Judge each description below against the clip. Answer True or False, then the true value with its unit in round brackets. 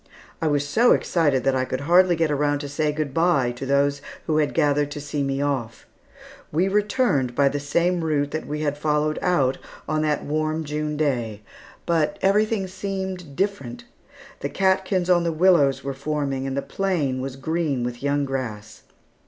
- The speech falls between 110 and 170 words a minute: False (180 wpm)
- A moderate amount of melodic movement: True (3.7 semitones)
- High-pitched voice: False (150 Hz)